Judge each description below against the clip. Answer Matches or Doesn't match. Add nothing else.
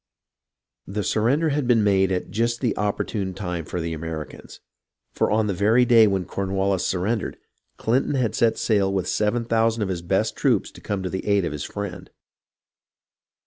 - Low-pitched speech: Matches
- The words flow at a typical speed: Matches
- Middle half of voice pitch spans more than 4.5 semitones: Doesn't match